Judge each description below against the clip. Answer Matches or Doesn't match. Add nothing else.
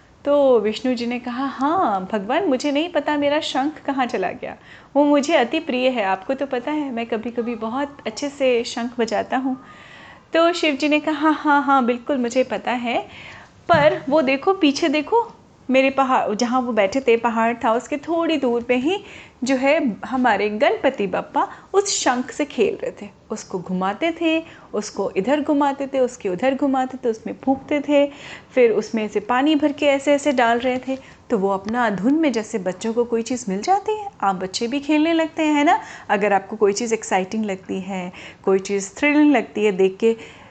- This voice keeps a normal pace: Doesn't match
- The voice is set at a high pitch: Matches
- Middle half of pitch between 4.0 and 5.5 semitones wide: Matches